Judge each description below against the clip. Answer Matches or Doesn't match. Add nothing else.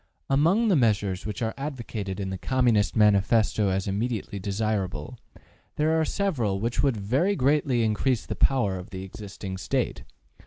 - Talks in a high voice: Doesn't match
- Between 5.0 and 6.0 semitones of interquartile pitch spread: Matches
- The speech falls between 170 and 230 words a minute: Doesn't match